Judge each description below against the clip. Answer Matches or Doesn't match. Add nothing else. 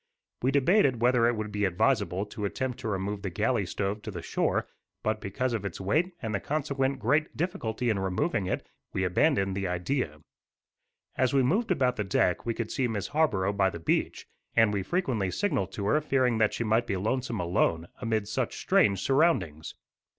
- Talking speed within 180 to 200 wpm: Matches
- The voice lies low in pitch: Matches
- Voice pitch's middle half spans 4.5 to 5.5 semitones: Matches